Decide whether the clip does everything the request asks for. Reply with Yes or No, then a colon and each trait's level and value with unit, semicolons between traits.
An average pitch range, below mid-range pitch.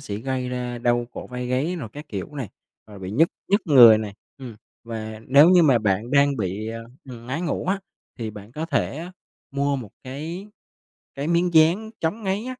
No: wide, 6.0 semitones; low, 130 Hz